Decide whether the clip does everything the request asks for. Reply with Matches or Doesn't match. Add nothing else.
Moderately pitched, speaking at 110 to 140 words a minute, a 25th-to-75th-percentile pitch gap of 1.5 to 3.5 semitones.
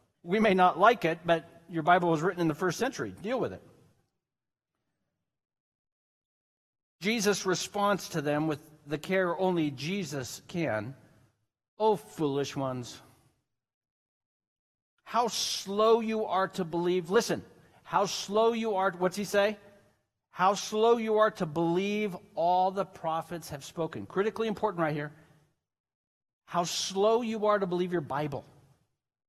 Doesn't match